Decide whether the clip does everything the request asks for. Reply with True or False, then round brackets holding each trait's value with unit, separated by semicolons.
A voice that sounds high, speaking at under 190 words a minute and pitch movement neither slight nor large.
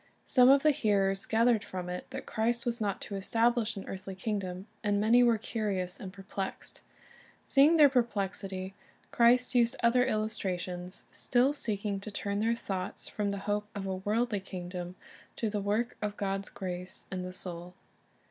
True (205 Hz; 165 wpm; 3.6 semitones)